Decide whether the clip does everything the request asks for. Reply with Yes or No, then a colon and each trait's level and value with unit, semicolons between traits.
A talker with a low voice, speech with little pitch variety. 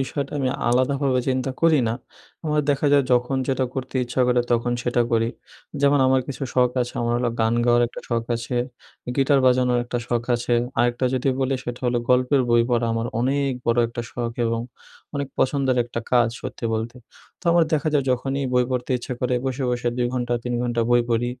Yes: low, 125 Hz; narrow, 1.9 semitones